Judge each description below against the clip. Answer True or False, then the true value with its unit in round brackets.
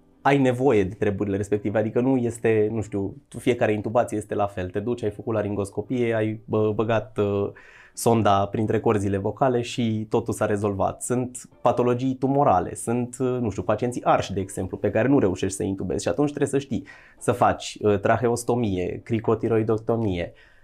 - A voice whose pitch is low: True (110 Hz)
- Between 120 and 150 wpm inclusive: False (160 wpm)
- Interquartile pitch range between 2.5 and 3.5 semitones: True (2.8 semitones)